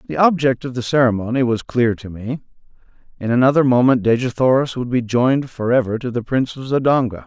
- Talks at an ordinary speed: Yes, average, 190 wpm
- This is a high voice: No, low, 125 Hz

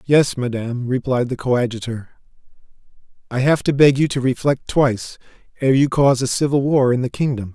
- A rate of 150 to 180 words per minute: Yes, average, 175 wpm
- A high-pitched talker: No, low, 130 Hz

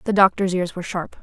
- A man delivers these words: No, female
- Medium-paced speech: No, fast, 245 wpm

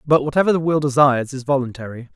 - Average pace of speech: Yes, average, 195 wpm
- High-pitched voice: No, medium, 140 Hz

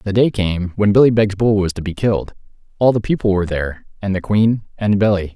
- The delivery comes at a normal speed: No, fast, 235 wpm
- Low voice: Yes, low, 100 Hz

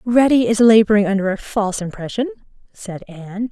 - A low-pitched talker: No, high, 215 Hz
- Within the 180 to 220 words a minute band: No, average, 155 wpm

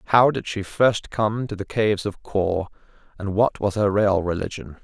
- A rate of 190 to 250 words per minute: Yes, average, 200 wpm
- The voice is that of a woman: No, male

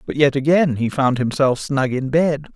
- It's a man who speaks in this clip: Yes, male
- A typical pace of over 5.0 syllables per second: No, 4.7 syllables/s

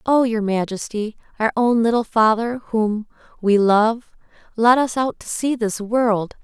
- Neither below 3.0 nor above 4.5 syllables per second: Yes, 4.0 syllables/s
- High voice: Yes, high, 225 Hz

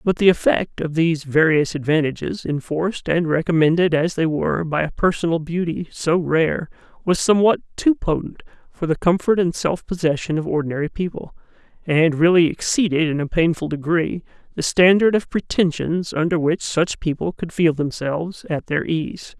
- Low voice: No, medium, 165 Hz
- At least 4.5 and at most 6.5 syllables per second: Yes, 5.1 syllables/s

